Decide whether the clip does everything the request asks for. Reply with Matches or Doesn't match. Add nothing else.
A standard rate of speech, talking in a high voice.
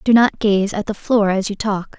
Doesn't match